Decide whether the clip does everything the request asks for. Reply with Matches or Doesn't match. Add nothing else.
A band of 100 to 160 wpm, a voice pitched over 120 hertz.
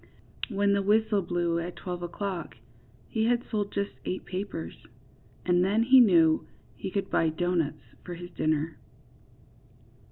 Matches